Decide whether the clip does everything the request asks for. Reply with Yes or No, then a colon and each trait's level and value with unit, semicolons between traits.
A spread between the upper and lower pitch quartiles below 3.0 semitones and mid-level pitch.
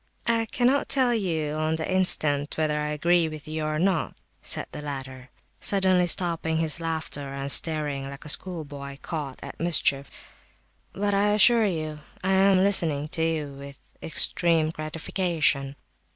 No: average, 4.0 semitones; medium, 160 Hz